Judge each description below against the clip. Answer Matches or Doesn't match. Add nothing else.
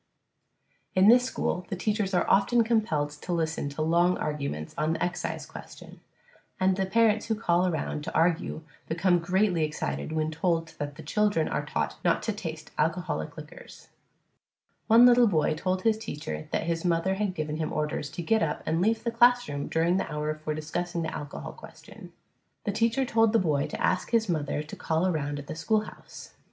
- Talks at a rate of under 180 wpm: Doesn't match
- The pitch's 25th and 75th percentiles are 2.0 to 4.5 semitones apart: Doesn't match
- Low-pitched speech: Doesn't match